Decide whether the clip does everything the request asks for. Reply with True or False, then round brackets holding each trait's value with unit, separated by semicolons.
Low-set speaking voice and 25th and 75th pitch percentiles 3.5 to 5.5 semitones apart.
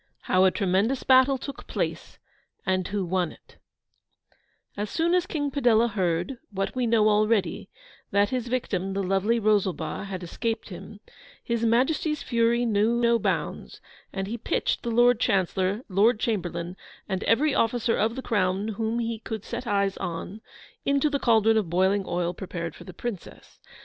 False (215 Hz; 3.8 semitones)